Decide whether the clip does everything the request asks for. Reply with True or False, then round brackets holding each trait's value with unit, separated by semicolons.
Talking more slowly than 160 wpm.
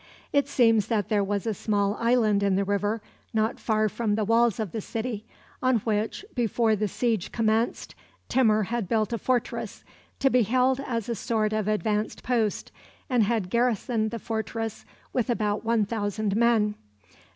False (170 wpm)